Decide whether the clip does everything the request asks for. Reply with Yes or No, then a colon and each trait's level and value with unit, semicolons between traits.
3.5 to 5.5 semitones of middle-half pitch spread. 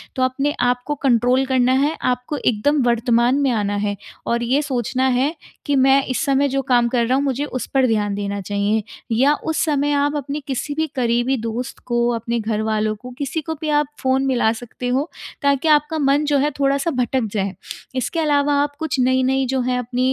No: average, 3.0 semitones